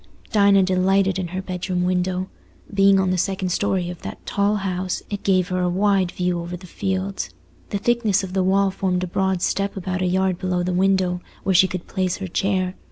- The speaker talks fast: Yes, fast, 210 wpm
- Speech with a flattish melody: Yes, narrow, 1.3 semitones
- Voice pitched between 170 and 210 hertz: Yes, medium, 185 Hz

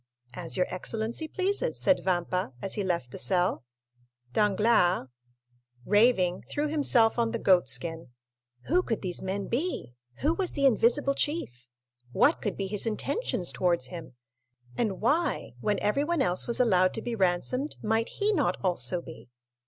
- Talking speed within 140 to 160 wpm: Yes, average, 155 wpm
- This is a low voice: No, high, 210 Hz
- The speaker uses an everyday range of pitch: No, wide, 7.4 semitones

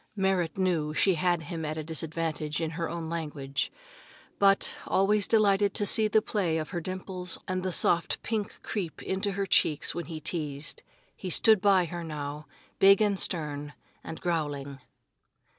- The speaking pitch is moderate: Yes, medium, 170 Hz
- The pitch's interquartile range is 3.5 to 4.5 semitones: Yes, average, 3.8 semitones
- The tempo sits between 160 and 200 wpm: Yes, average, 165 wpm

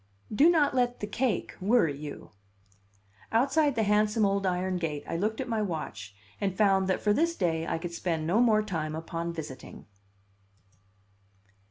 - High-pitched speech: Yes, high, 195 Hz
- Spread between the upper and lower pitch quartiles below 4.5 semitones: No, average, 5.3 semitones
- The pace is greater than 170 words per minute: No, average, 165 wpm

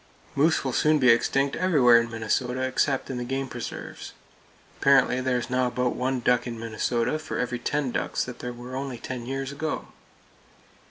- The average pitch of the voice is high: No, low, 125 Hz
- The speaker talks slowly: No, average, 180 wpm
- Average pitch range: No, narrow, 1.9 semitones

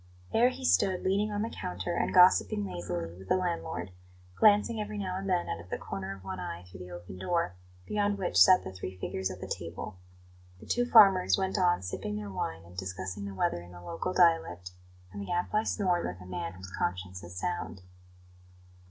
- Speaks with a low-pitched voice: Yes, low, 100 Hz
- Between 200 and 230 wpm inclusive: Yes, fast, 205 wpm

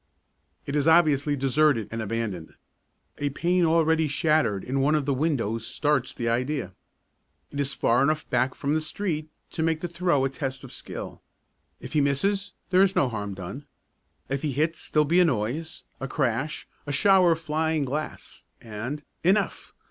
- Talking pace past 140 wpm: Yes, average, 170 wpm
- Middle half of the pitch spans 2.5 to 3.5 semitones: No, average, 3.9 semitones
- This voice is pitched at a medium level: Yes, medium, 145 Hz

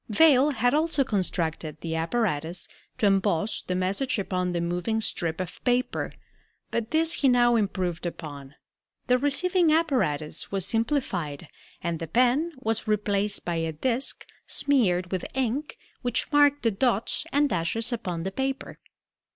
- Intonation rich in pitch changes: Yes, wide, 7.1 semitones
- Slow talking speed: No, average, 145 wpm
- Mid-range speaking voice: No, high, 215 Hz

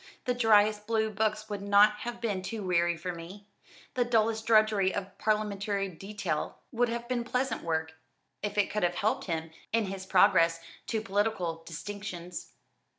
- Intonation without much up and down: No, average, 3.0 semitones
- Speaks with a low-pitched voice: No, high, 205 Hz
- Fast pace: No, average, 160 wpm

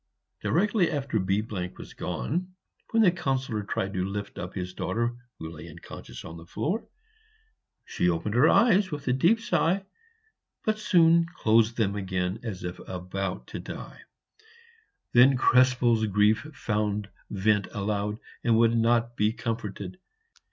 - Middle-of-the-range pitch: No, low, 110 Hz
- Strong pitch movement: Yes, wide, 6.1 semitones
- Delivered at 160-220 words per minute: No, average, 145 wpm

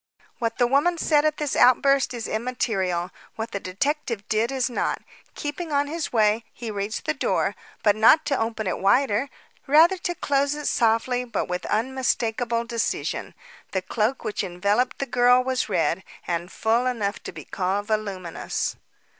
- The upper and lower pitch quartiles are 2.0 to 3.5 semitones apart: No, average, 4.8 semitones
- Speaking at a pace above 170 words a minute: No, average, 165 wpm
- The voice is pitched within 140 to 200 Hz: No, high, 235 Hz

